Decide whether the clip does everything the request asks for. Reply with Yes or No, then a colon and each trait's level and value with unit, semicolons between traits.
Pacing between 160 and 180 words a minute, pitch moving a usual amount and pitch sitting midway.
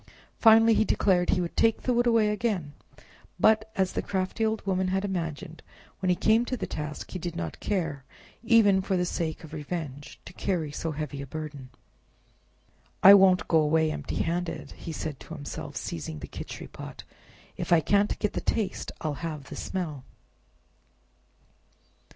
Yes: average, 175 wpm; average, 4.7 semitones; medium, 180 Hz